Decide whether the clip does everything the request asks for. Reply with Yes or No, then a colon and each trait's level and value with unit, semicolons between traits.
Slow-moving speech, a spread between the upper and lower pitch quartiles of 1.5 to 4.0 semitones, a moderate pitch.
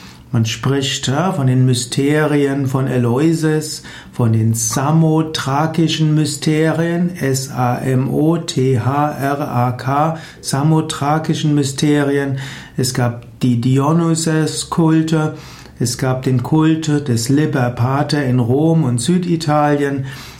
Yes: slow, 85 wpm; average, 3.2 semitones; medium, 145 Hz